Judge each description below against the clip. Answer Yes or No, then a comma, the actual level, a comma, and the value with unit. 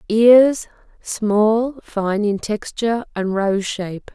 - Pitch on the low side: No, high, 215 Hz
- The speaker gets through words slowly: Yes, slow, 100 wpm